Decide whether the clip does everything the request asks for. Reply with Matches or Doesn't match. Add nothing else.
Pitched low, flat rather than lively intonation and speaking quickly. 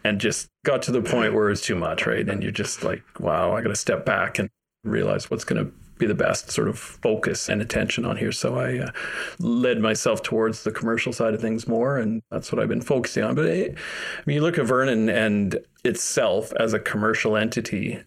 Matches